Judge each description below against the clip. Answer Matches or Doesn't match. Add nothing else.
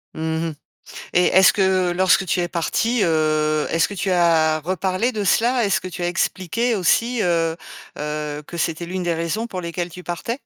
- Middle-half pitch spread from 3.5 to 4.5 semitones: Doesn't match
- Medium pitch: Matches